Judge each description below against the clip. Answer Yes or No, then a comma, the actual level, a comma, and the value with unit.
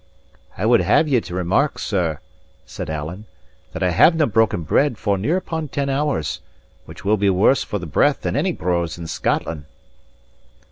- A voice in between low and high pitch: No, low, 100 Hz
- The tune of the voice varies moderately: No, wide, 8.1 semitones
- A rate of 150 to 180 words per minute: Yes, average, 175 wpm